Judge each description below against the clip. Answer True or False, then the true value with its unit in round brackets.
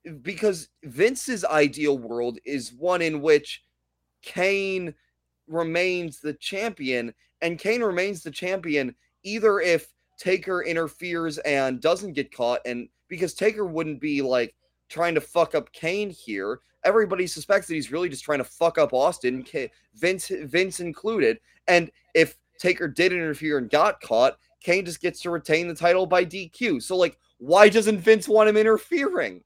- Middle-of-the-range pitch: True (170 Hz)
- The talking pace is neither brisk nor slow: True (155 wpm)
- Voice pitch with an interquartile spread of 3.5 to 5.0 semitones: True (4.3 semitones)